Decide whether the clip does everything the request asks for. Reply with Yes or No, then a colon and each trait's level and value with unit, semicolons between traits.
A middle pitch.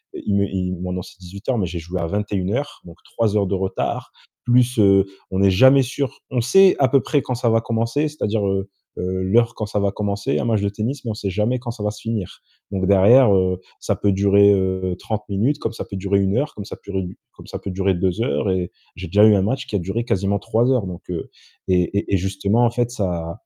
No: low, 100 Hz